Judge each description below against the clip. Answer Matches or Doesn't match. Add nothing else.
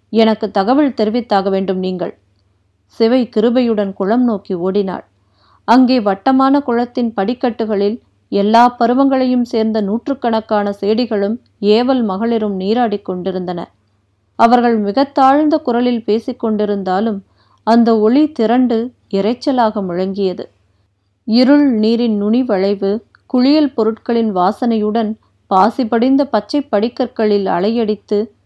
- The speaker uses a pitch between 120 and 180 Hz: Doesn't match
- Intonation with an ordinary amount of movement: Matches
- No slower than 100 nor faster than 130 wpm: Doesn't match